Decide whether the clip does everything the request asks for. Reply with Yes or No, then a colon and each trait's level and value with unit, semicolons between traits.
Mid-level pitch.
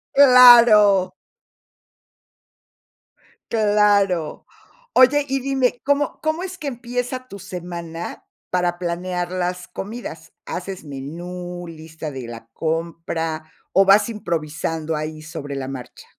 Yes: medium, 180 Hz